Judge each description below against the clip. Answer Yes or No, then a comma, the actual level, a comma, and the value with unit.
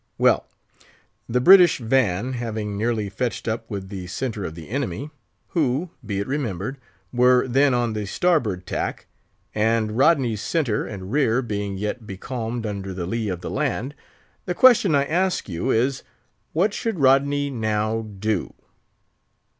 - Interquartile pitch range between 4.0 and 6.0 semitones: Yes, average, 4.9 semitones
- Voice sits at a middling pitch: No, low, 115 Hz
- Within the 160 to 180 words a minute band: No, average, 140 wpm